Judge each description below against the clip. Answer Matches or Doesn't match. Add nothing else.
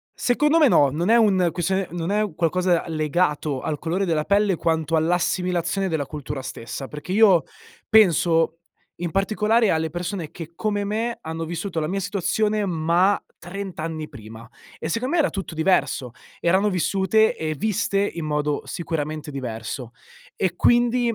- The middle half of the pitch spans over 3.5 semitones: Matches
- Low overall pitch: Doesn't match